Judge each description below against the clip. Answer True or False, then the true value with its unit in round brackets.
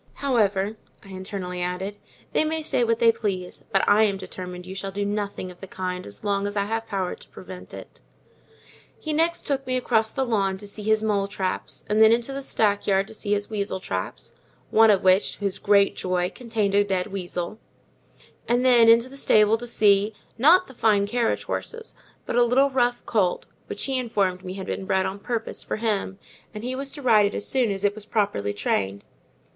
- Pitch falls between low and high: False (205 Hz)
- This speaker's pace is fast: True (215 wpm)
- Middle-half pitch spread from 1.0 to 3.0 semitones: False (3.4 semitones)